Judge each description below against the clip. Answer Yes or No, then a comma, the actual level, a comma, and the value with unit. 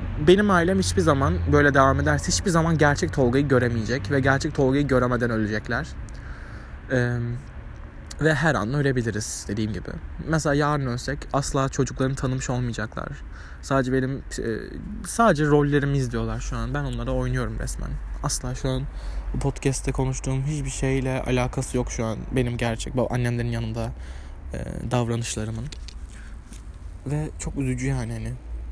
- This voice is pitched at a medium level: No, low, 125 Hz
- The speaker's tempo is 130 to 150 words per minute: Yes, fast, 140 wpm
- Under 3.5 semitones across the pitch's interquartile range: No, average, 4.0 semitones